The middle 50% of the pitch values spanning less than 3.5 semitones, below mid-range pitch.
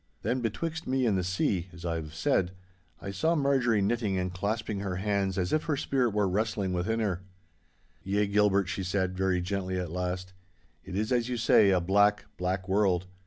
Yes: average, 3.0 semitones; low, 100 Hz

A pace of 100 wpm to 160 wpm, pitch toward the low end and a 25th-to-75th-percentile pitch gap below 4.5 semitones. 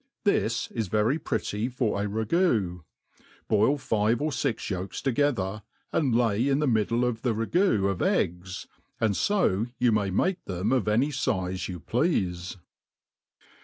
No: average, 150 wpm; low, 110 Hz; average, 5.0 semitones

